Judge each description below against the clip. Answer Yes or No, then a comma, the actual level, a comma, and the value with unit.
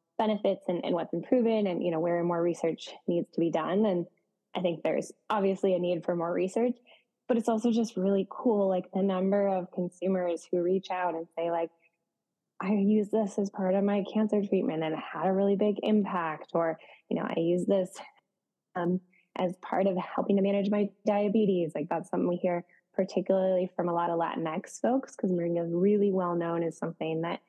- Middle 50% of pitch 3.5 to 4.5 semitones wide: No, average, 3.1 semitones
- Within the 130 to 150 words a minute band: No, fast, 205 wpm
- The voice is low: No, medium, 185 Hz